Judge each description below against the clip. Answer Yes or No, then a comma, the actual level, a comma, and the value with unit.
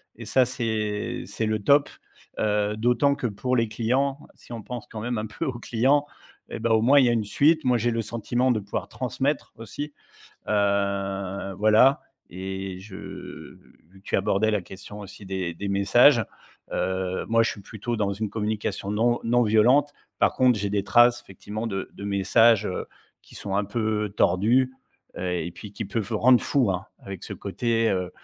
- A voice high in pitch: No, low, 110 Hz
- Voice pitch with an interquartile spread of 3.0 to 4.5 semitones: Yes, average, 3.4 semitones